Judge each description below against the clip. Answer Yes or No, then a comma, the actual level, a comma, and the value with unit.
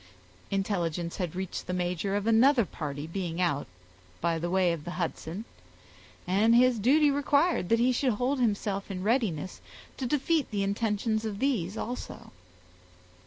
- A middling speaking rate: Yes, average, 155 wpm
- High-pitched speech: Yes, high, 200 Hz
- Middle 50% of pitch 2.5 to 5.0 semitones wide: No, wide, 5.4 semitones